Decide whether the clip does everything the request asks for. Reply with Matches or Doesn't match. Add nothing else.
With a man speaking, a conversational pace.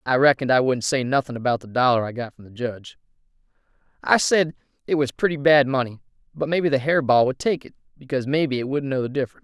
Doesn't match